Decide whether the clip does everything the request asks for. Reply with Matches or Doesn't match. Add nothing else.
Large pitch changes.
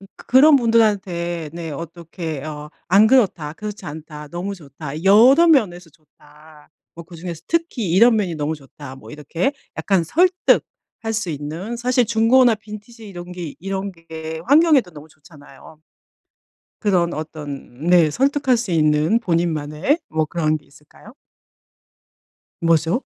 Matches